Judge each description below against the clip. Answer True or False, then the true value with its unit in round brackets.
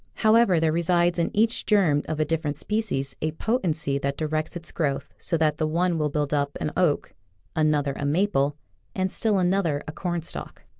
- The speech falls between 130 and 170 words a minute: False (185 wpm)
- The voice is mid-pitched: True (160 Hz)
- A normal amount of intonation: True (3.5 semitones)